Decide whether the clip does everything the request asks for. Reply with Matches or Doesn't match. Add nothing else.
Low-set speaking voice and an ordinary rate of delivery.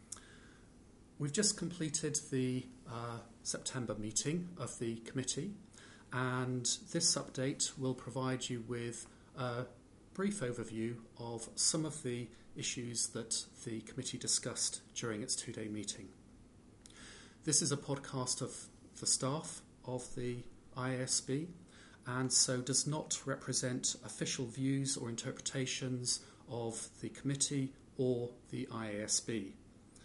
Doesn't match